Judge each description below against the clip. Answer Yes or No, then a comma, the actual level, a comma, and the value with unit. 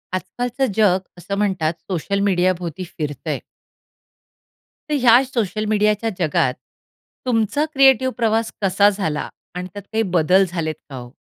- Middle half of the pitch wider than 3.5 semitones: Yes, average, 4.3 semitones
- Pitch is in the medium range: No, high, 200 Hz